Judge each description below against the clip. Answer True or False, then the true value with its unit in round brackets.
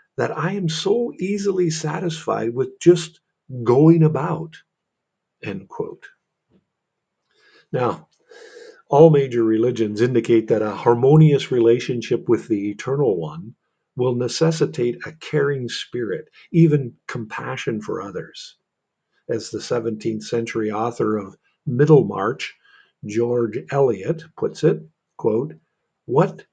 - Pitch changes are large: True (6.4 semitones)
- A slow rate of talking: True (105 wpm)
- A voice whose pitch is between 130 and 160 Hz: True (140 Hz)